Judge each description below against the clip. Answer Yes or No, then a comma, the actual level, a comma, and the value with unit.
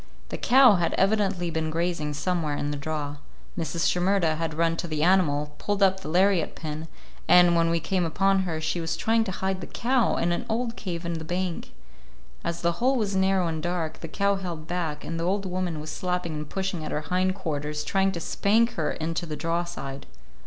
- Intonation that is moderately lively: Yes, average, 3.2 semitones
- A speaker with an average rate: No, fast, 215 wpm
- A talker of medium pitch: Yes, medium, 170 Hz